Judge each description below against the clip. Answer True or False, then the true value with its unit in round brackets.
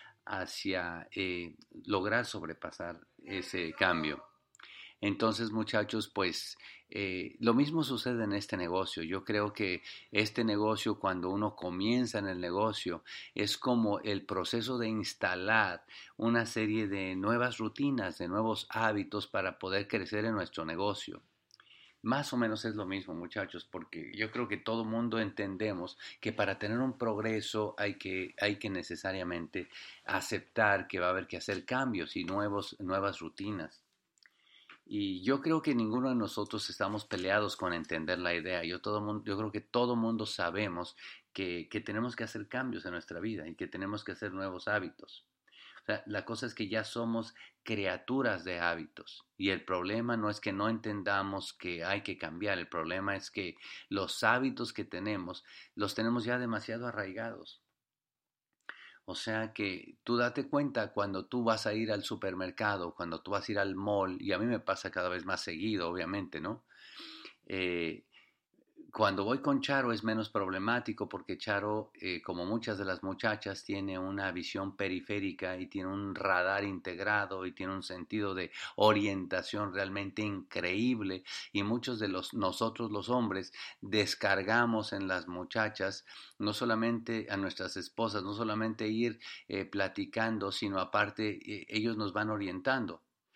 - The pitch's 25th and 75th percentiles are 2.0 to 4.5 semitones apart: True (2.7 semitones)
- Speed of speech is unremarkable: True (160 wpm)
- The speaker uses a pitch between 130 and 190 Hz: False (105 Hz)